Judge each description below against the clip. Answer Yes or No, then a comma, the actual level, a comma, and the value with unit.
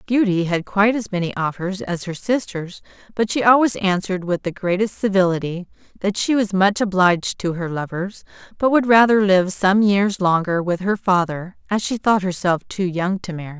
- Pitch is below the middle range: No, high, 190 Hz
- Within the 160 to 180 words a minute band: No, average, 190 wpm